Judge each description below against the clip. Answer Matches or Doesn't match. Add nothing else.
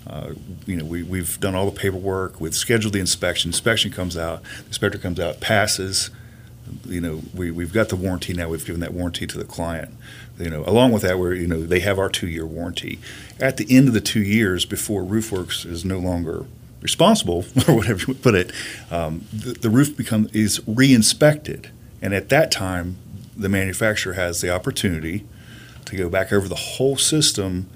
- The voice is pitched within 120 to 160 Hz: Doesn't match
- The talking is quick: Doesn't match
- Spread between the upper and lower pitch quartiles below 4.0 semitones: Doesn't match